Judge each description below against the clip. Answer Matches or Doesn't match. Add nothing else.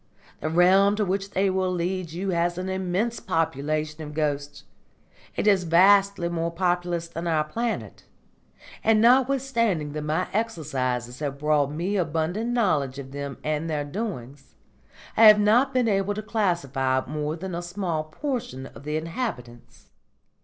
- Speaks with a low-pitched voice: Doesn't match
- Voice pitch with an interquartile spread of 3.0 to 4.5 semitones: Doesn't match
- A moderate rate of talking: Matches